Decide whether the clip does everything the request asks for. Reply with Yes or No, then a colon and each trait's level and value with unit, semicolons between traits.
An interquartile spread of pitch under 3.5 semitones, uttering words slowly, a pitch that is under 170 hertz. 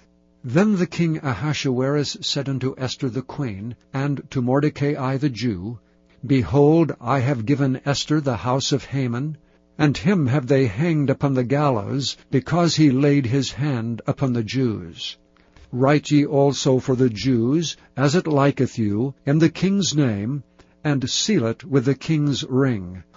No: average, 2.7 semitones; average, 155 wpm; low, 135 Hz